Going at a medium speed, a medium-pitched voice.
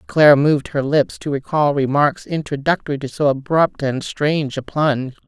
Yes: average, 170 wpm; medium, 145 Hz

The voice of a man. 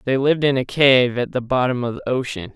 Yes: male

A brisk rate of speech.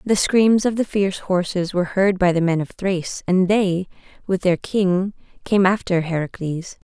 No: average, 180 wpm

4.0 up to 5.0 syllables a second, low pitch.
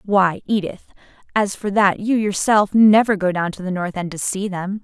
No: 4.8 syllables/s; high, 195 Hz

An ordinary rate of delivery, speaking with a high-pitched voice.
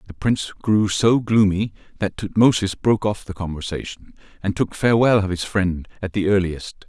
No: average, 175 wpm; low, 100 Hz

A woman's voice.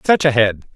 No: male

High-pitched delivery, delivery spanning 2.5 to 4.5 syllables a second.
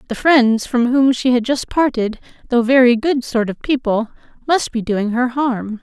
Yes: high, 245 Hz; 4.4 syllables/s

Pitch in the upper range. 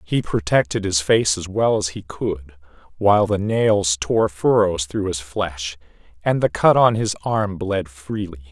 No: very low, 95 Hz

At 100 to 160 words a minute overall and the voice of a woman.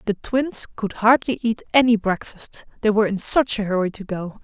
No: fast, 205 wpm; female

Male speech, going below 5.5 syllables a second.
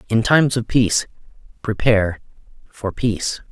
Yes: male; 5.2 syllables/s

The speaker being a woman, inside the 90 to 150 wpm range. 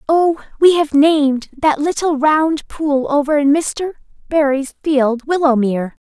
Yes: female; average, 140 wpm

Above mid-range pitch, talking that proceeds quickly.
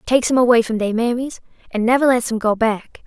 Yes: high, 235 Hz; fast, 235 wpm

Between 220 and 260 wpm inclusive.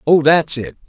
No: fast, 205 wpm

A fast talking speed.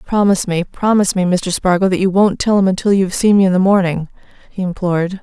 Yes: fast, 230 wpm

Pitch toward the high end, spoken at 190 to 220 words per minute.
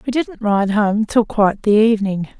Yes: high, 215 Hz; average, 200 wpm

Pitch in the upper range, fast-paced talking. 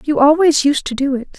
Yes: very high, 285 Hz; fast, 260 wpm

